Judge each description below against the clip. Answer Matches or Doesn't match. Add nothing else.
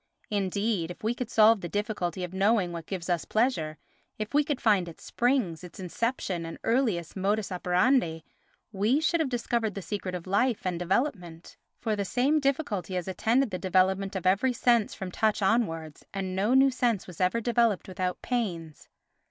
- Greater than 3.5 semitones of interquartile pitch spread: Matches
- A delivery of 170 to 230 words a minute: Matches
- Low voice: Doesn't match